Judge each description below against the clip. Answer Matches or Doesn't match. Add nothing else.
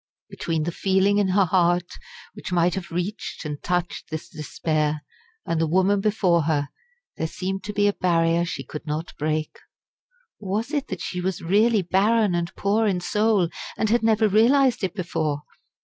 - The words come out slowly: Doesn't match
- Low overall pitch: Doesn't match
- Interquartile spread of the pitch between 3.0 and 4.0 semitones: Matches